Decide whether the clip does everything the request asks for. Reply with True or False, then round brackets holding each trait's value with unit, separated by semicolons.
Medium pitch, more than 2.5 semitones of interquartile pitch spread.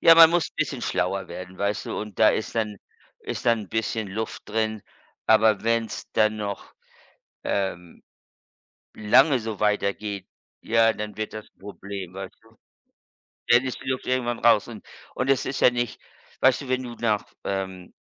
False (110 Hz; 2.9 semitones)